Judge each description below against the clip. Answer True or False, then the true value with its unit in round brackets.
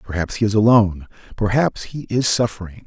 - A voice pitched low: True (110 Hz)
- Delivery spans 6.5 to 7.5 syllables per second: False (5.7 syllables/s)